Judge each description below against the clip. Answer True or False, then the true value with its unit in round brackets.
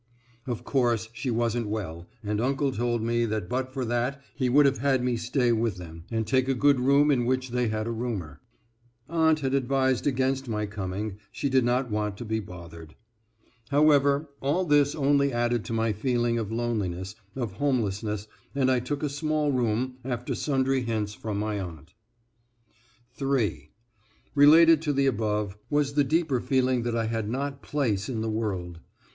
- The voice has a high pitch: False (120 Hz)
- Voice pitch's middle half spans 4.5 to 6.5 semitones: False (4.1 semitones)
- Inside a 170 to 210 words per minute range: True (175 wpm)